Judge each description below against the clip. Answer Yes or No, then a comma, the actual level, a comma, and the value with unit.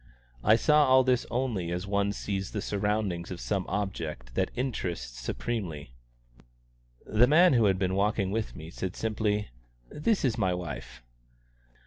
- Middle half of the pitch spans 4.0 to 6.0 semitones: Yes, average, 4.4 semitones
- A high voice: No, low, 100 Hz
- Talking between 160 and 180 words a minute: No, average, 150 wpm